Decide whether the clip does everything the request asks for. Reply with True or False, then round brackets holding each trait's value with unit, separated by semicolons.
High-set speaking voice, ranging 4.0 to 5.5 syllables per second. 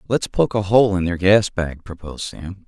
False (95 Hz; 4.8 syllables/s)